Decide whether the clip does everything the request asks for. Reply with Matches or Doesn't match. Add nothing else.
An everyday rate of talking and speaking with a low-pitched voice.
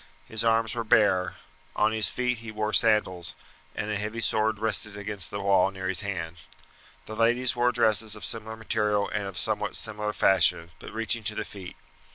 Matches